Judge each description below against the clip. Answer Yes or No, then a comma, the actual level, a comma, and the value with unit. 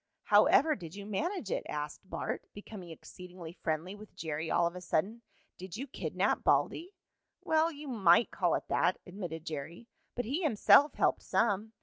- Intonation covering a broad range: Yes, wide, 6.0 semitones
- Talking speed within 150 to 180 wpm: Yes, average, 175 wpm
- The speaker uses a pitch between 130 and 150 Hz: No, high, 195 Hz